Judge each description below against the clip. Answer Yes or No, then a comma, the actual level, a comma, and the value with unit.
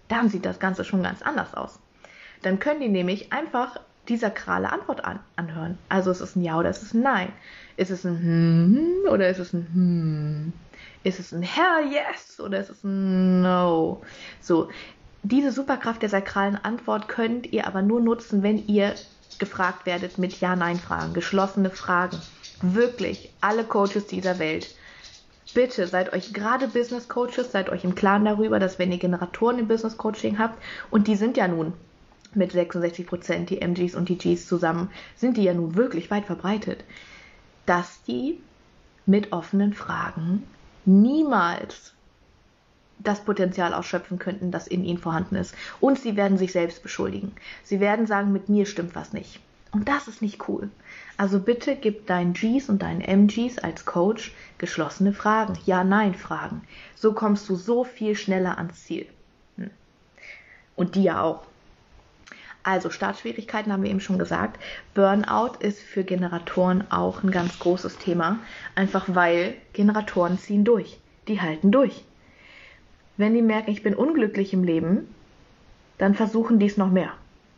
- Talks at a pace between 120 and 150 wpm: No, average, 165 wpm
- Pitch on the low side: No, high, 195 Hz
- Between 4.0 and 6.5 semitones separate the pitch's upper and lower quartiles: No, average, 3.2 semitones